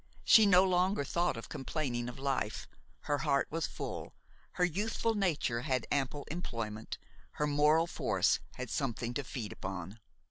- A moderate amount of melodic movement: No, wide, 6.2 semitones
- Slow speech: No, average, 150 wpm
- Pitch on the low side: No, medium, 145 Hz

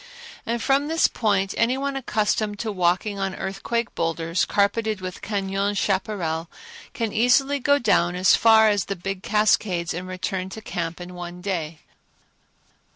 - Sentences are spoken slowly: No, average, 155 wpm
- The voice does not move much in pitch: No, average, 3.5 semitones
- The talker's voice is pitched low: No, high, 200 Hz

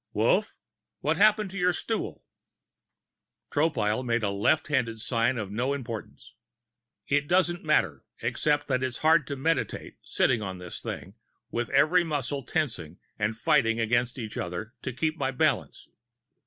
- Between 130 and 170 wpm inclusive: Yes, average, 150 wpm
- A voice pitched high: No, low, 130 Hz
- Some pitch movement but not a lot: No, wide, 5.7 semitones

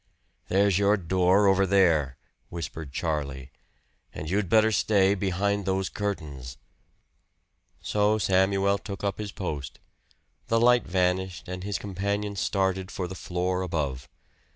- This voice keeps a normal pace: No, slow, 130 wpm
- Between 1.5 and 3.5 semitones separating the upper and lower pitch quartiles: Yes, narrow, 2.5 semitones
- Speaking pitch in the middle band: No, very low, 95 Hz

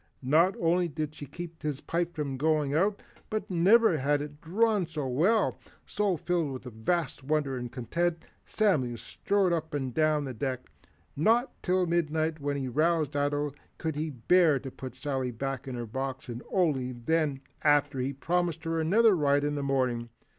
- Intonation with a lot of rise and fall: No, average, 4.2 semitones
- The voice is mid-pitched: Yes, medium, 150 Hz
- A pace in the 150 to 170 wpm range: No, average, 180 wpm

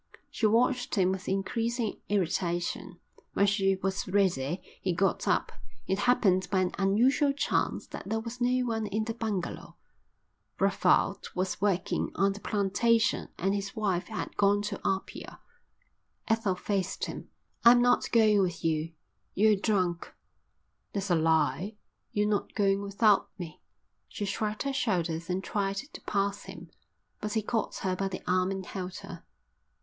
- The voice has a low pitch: No, high, 200 Hz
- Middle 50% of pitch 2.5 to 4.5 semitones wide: Yes, average, 2.8 semitones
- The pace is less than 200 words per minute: Yes, average, 155 wpm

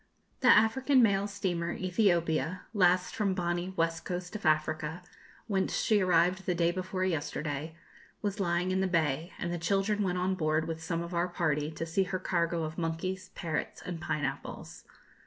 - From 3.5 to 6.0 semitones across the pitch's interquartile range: No, narrow, 2.5 semitones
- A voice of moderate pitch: Yes, medium, 175 Hz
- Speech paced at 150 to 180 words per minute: Yes, average, 175 wpm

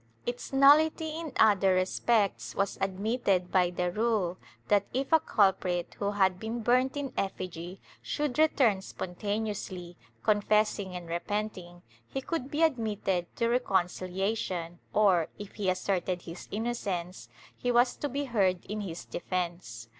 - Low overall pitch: No, high, 200 Hz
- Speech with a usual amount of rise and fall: Yes, average, 4.7 semitones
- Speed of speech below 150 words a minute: Yes, average, 140 wpm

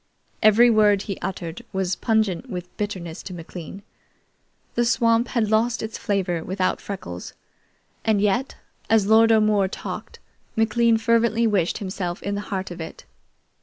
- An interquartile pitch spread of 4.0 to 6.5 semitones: No, average, 3.2 semitones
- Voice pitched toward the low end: No, high, 205 Hz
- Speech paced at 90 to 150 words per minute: Yes, average, 145 wpm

